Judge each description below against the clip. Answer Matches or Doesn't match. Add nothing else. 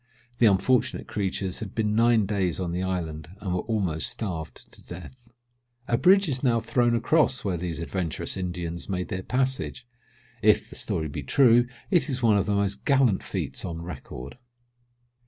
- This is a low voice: Matches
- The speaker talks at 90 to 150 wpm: Doesn't match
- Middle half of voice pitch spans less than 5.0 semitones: Doesn't match